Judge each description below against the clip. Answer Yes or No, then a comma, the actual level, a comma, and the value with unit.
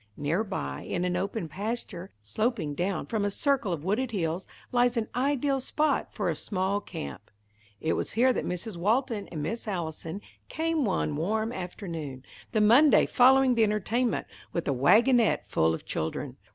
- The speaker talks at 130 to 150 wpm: No, average, 165 wpm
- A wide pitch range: Yes, wide, 6.0 semitones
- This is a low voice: No, high, 205 Hz